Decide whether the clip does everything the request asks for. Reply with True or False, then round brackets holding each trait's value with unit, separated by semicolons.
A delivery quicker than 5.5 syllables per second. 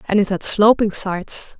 False (4.9 syllables/s)